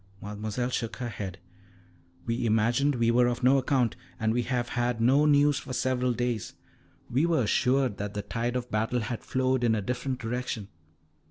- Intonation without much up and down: Yes, narrow, 2.3 semitones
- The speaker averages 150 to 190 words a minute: Yes, average, 180 wpm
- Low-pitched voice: Yes, low, 120 Hz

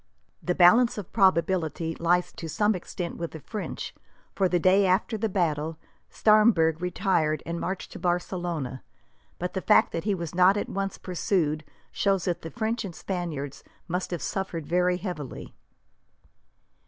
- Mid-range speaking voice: Yes, medium, 180 Hz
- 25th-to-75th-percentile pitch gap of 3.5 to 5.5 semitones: No, average, 2.8 semitones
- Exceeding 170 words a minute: No, average, 155 wpm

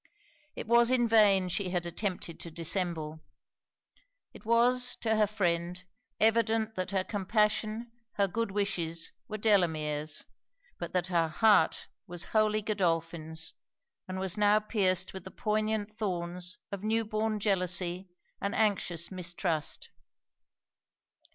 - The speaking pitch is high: Yes, high, 195 Hz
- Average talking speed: No, slow, 125 wpm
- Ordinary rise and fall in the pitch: Yes, average, 3.7 semitones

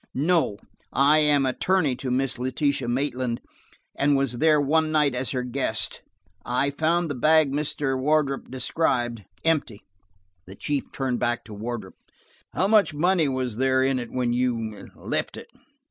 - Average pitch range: Yes, average, 3.5 semitones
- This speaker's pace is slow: No, average, 155 wpm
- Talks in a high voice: No, low, 135 Hz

